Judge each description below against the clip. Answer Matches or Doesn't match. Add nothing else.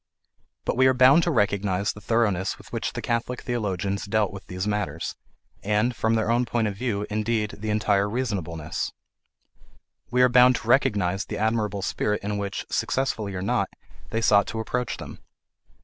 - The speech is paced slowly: Doesn't match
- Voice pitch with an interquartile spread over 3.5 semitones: Doesn't match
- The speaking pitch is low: Matches